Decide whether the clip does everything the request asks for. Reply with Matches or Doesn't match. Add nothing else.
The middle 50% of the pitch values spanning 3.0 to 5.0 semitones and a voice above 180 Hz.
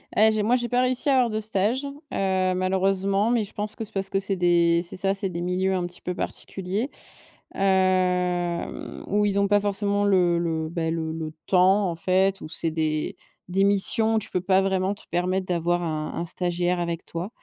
Doesn't match